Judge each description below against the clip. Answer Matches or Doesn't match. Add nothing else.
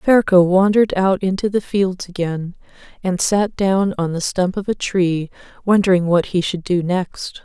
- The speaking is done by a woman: Matches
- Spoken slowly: Doesn't match